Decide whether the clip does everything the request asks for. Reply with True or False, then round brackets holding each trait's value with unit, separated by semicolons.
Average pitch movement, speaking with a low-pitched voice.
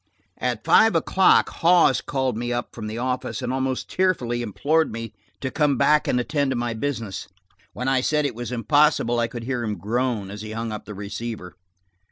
True (3.6 semitones; 120 Hz)